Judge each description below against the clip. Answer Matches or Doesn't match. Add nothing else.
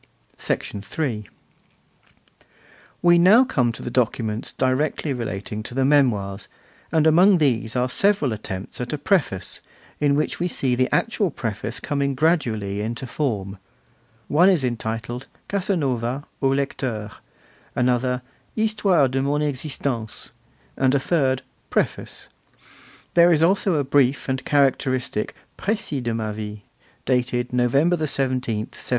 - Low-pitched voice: Matches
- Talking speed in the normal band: Doesn't match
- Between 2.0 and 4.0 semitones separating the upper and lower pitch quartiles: Doesn't match